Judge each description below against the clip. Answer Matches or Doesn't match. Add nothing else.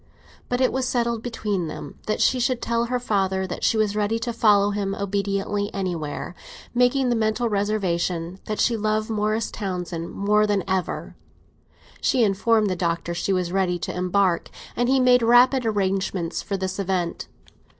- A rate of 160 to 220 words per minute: Matches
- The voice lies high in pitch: Matches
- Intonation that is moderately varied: Matches